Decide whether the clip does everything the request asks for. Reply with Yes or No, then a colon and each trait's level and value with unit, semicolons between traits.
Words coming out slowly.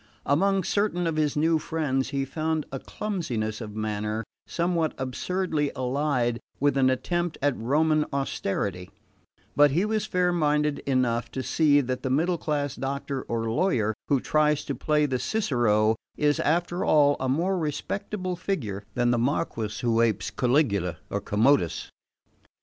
No: average, 150 wpm